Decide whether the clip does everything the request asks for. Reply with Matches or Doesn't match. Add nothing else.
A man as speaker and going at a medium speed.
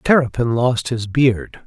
Matches